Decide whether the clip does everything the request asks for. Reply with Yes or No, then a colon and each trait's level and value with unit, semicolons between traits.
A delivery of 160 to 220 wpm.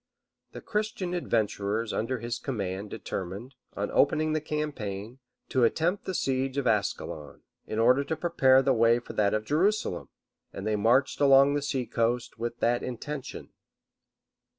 No: average, 150 wpm